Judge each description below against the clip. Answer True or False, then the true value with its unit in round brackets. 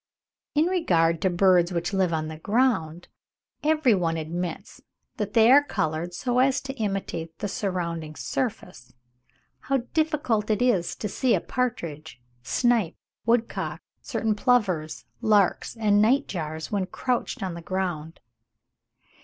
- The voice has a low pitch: False (195 Hz)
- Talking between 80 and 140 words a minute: True (135 wpm)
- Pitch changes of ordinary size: False (6.3 semitones)